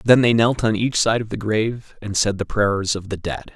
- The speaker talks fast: Yes, fast, 270 wpm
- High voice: No, low, 105 Hz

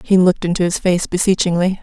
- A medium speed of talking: Yes, average, 195 wpm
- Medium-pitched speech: Yes, medium, 180 Hz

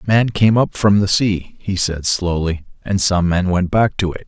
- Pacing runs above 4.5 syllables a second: No, 4.4 syllables/s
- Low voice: Yes, very low, 95 Hz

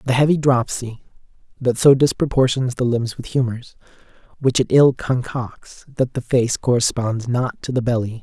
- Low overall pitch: Yes, low, 125 Hz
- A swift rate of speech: No, average, 160 wpm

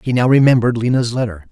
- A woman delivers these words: No, male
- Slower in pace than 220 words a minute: Yes, average, 200 wpm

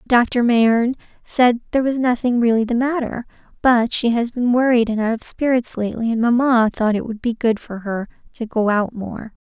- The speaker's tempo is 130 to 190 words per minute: No, fast, 205 wpm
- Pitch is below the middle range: No, high, 235 Hz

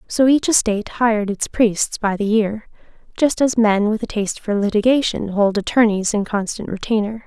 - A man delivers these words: No, female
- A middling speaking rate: Yes, average, 180 wpm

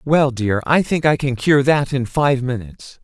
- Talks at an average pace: No, fast, 220 wpm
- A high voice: No, low, 135 Hz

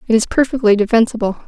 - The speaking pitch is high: Yes, high, 225 Hz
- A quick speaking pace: No, average, 165 wpm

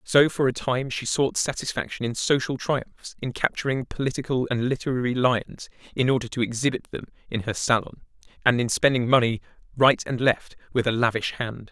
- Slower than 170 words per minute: No, average, 180 wpm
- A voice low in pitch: Yes, low, 125 Hz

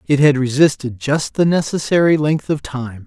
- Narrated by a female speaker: No, male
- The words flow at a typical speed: Yes, average, 175 wpm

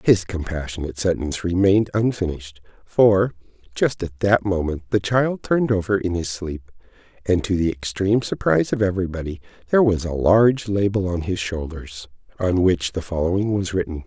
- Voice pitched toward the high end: No, very low, 95 Hz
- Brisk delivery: No, average, 160 wpm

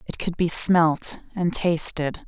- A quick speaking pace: No, average, 160 wpm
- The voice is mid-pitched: Yes, medium, 170 Hz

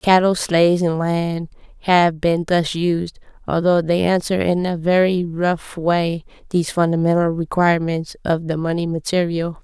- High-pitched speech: No, medium, 170 Hz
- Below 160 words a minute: Yes, average, 145 wpm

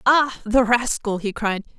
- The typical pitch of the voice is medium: No, high, 230 Hz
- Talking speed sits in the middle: Yes, average, 170 wpm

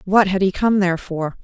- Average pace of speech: No, fast, 250 wpm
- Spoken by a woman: Yes, female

